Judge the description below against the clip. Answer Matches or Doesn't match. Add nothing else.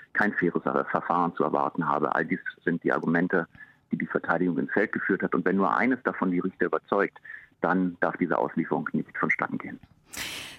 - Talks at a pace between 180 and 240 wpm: Matches